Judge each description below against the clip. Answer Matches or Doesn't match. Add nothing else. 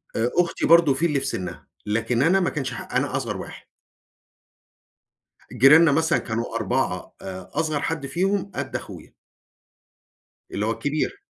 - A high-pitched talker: Doesn't match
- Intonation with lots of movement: Matches